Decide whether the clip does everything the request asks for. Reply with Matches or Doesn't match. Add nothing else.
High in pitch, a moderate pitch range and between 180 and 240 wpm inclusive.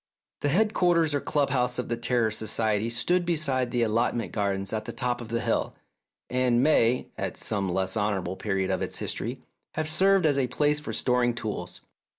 Doesn't match